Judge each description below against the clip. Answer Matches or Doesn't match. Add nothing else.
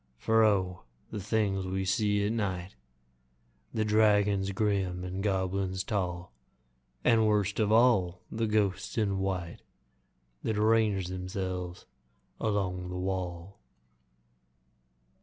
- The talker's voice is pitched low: Matches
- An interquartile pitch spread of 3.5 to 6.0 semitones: Doesn't match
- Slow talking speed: Matches